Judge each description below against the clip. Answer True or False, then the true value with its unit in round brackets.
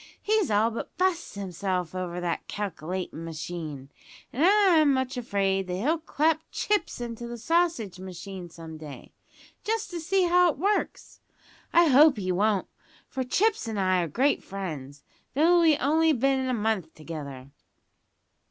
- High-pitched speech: True (220 Hz)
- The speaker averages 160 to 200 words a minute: False (150 wpm)